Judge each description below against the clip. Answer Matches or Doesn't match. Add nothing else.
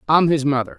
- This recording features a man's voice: Matches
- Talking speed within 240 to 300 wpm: Doesn't match